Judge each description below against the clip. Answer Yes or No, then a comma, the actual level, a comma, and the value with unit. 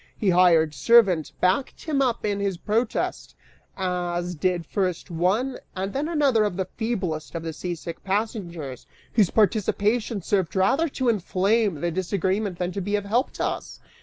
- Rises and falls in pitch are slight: No, average, 3.9 semitones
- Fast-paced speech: No, average, 165 wpm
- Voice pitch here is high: Yes, high, 195 Hz